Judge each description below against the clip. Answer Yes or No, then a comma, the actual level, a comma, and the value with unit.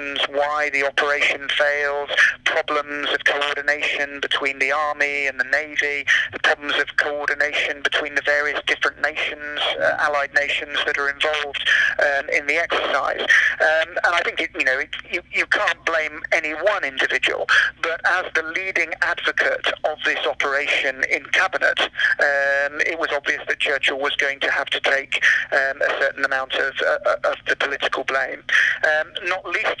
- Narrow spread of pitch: Yes, narrow, 1.4 semitones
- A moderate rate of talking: Yes, average, 165 wpm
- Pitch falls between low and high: Yes, medium, 145 Hz